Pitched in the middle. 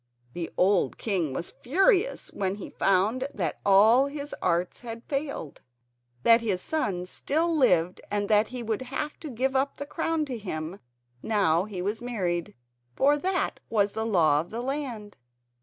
No: high, 220 Hz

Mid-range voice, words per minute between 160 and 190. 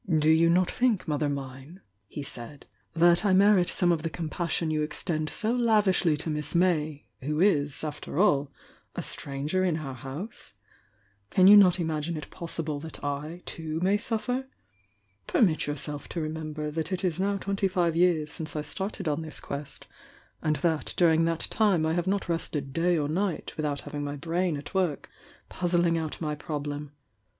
Yes: medium, 160 Hz; average, 180 wpm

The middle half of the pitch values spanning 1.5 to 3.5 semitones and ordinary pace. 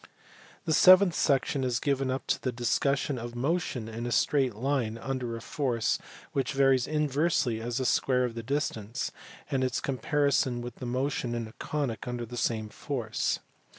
Yes: average, 2.9 semitones; average, 170 wpm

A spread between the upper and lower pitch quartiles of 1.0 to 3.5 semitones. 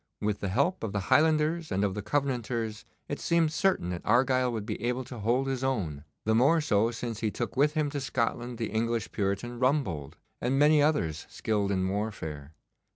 No: average, 5.0 semitones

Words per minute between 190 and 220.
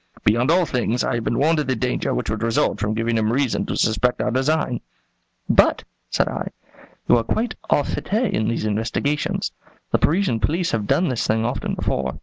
Yes: average, 200 wpm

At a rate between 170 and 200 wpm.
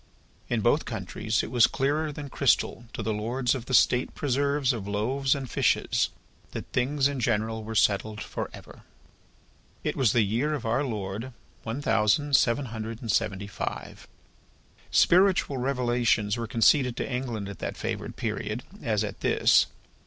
No: average, 160 wpm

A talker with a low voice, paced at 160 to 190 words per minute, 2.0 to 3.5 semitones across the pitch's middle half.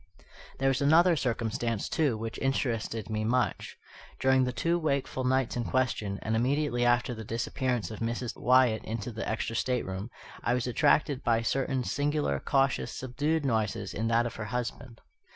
Yes: low, 125 Hz; average, 165 wpm; average, 2.9 semitones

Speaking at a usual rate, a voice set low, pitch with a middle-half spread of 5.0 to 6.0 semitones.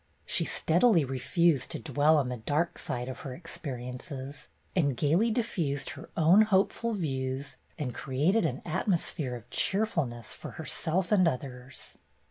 No: average, 150 wpm; medium, 150 Hz; average, 5.3 semitones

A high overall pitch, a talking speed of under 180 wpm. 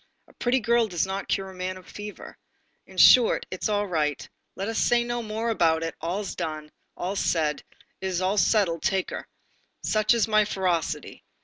No: high, 195 Hz; average, 185 wpm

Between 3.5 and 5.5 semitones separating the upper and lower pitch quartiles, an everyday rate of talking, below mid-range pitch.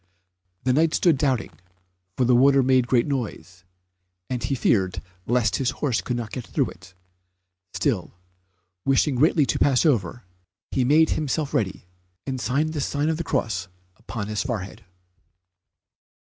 Yes: average, 4.0 semitones; average, 155 wpm; low, 125 Hz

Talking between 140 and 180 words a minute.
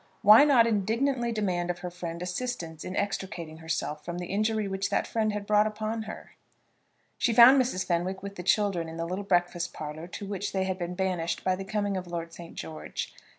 No: fast, 205 wpm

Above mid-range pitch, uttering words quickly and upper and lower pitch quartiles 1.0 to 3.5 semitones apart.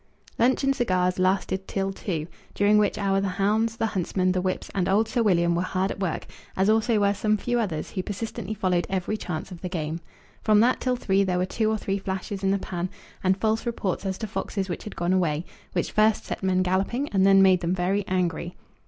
Yes: high, 195 Hz; fast, 225 wpm; narrow, 2.6 semitones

